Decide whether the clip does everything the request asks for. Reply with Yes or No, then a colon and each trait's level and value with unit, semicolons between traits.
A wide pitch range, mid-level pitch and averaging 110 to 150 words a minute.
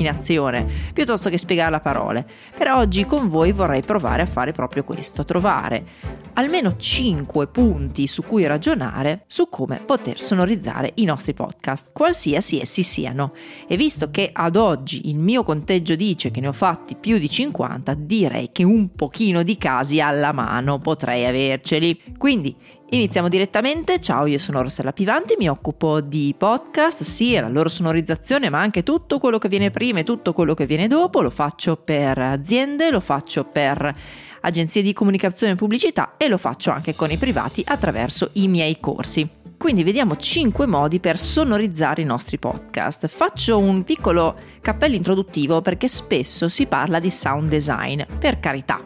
No: wide, 6.4 semitones; medium, 170 Hz; average, 165 wpm